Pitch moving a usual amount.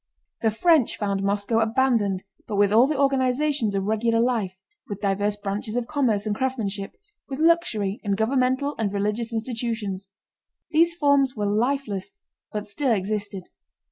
Yes: average, 4.4 semitones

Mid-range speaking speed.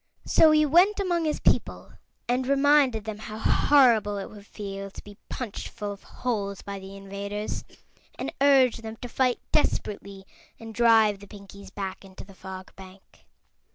Yes: average, 165 wpm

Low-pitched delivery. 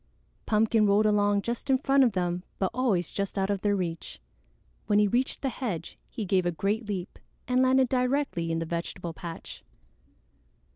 No: high, 205 Hz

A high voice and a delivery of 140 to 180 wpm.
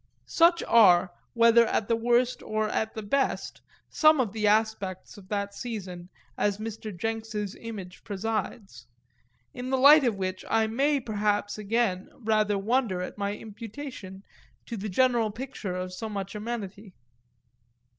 Yes: high, 215 Hz; average, 145 wpm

